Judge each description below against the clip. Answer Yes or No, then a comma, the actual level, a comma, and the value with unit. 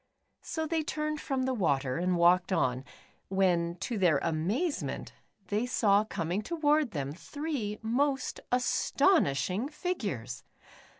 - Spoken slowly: Yes, slow, 120 wpm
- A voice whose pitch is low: No, high, 210 Hz